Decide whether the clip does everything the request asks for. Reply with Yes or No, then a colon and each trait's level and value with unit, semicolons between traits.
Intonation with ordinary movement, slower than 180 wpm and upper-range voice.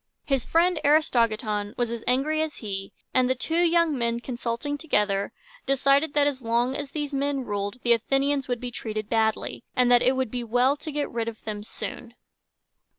No: average, 3.8 semitones; average, 190 wpm; very high, 250 Hz